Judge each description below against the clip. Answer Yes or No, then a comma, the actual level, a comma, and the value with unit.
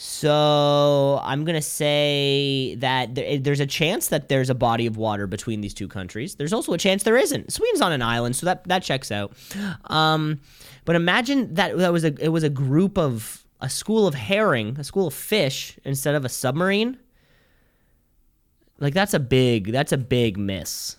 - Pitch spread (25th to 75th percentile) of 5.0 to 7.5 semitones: Yes, wide, 5.5 semitones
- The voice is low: No, medium, 145 Hz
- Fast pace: No, average, 185 wpm